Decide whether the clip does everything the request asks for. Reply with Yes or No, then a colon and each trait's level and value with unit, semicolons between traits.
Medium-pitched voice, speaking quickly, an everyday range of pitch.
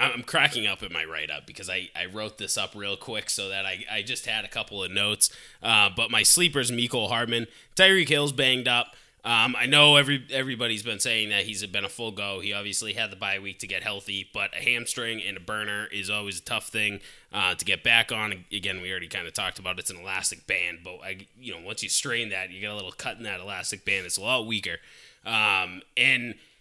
No: low, 105 Hz; fast, 240 wpm; average, 3.3 semitones